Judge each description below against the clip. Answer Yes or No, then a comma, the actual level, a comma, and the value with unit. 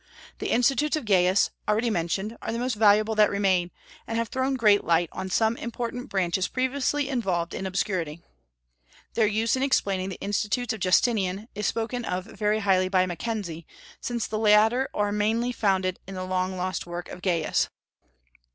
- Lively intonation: No, average, 3.8 semitones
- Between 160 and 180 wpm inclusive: Yes, average, 170 wpm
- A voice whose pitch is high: Yes, high, 210 Hz